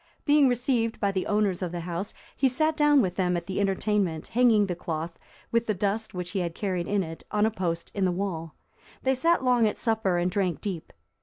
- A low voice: No, high, 200 Hz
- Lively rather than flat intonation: No, average, 4.3 semitones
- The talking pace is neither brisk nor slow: No, fast, 225 wpm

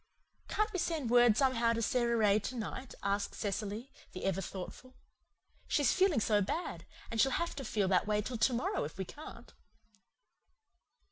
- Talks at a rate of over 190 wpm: No, average, 175 wpm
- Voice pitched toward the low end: No, high, 230 Hz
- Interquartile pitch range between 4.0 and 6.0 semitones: Yes, average, 4.3 semitones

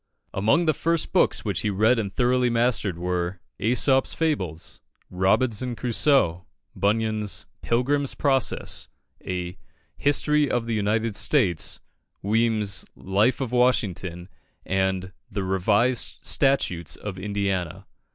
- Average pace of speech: No, slow, 110 wpm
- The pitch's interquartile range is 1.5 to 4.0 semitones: No, average, 4.8 semitones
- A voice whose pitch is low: Yes, low, 110 Hz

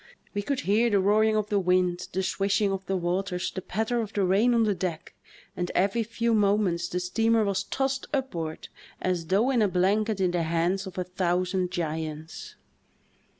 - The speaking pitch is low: No, high, 195 Hz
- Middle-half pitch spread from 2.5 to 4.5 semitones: Yes, average, 3.3 semitones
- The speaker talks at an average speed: Yes, average, 190 wpm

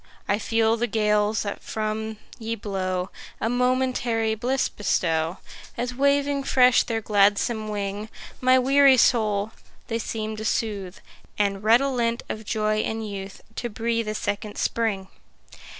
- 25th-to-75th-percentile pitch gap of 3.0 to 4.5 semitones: No, narrow, 2.6 semitones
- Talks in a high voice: Yes, high, 220 Hz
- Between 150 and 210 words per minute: No, slow, 135 wpm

